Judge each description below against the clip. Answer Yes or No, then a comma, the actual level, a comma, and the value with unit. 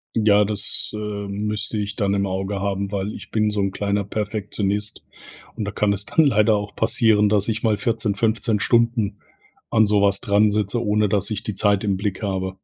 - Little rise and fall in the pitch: Yes, narrow, 1.2 semitones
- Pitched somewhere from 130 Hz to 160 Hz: No, low, 105 Hz